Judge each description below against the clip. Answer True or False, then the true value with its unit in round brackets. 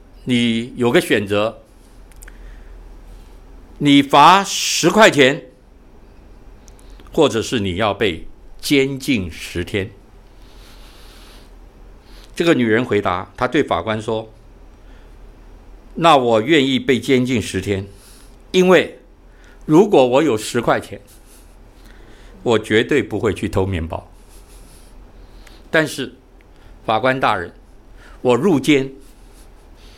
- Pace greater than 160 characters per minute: False (135 characters per minute)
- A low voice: True (100 Hz)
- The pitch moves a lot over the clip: True (6.7 semitones)